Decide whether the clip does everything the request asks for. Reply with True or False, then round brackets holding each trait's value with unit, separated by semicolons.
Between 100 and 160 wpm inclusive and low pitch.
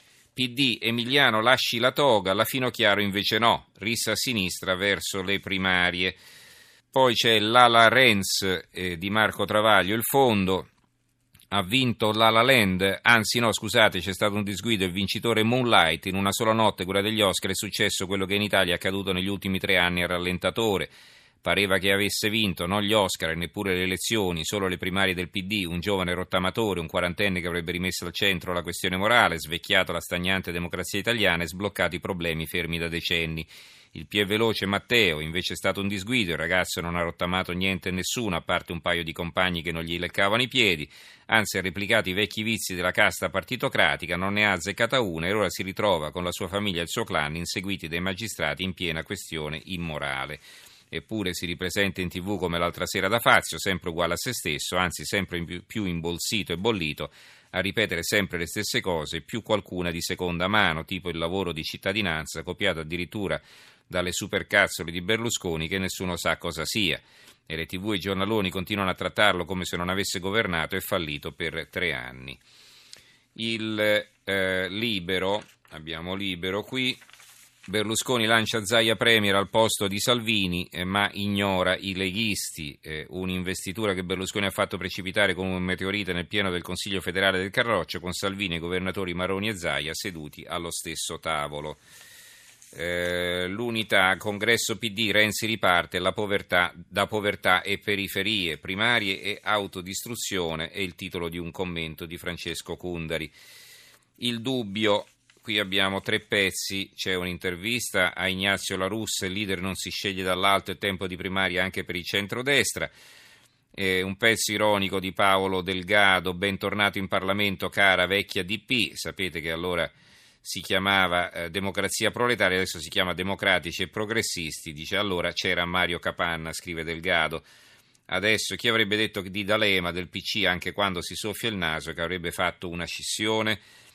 False (170 wpm; 95 Hz)